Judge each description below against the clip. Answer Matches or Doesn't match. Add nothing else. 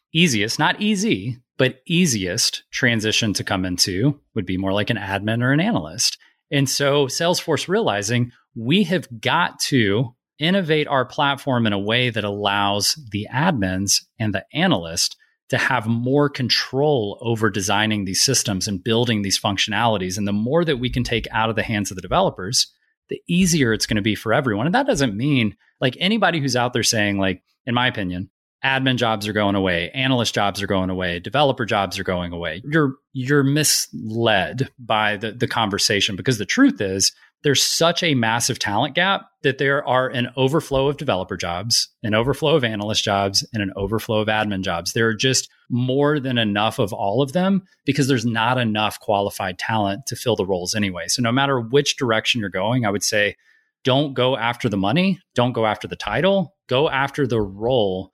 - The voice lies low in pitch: Matches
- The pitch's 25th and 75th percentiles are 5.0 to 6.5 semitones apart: Matches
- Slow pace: Doesn't match